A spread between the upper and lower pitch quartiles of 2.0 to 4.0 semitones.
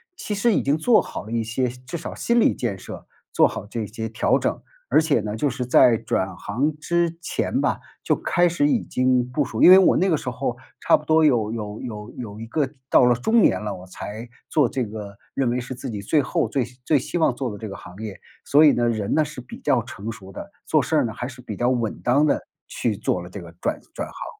No: wide, 5.4 semitones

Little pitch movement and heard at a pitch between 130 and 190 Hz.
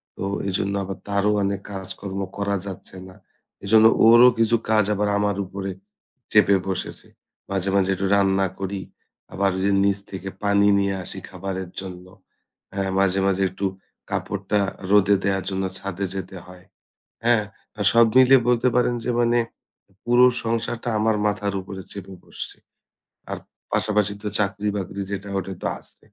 No: narrow, 1.5 semitones; low, 100 Hz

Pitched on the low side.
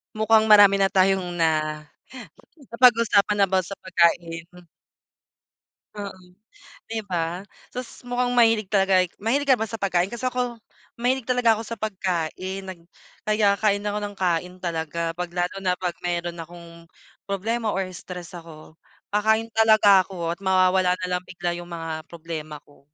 No: high, 190 Hz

